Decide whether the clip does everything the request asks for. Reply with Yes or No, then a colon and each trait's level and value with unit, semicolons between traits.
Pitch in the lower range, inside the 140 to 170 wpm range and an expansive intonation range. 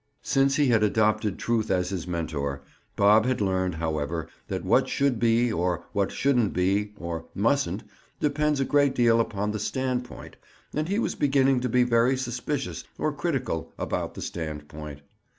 Yes: low, 110 Hz; average, 160 wpm; wide, 6.9 semitones